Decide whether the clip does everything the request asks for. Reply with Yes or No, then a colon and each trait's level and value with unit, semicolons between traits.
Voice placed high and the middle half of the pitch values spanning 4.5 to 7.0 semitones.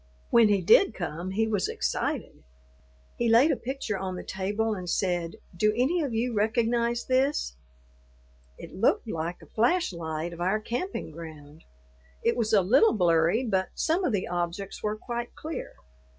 Yes: high, 210 Hz; average, 5.3 semitones